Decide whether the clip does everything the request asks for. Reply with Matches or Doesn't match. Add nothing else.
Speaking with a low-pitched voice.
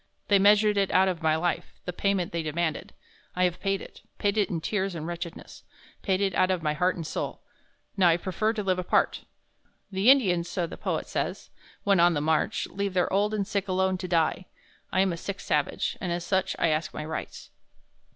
Doesn't match